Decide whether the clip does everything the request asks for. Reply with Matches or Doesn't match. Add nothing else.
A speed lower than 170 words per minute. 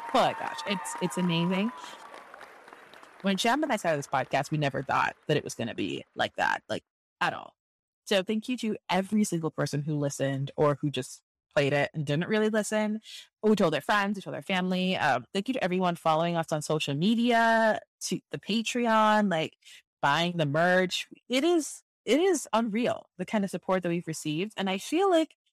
Doesn't match